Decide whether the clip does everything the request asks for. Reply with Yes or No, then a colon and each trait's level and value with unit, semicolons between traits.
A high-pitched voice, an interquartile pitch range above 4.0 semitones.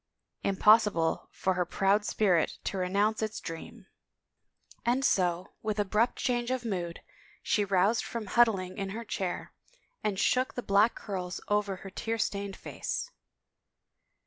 No: high, 200 Hz; average, 3.1 semitones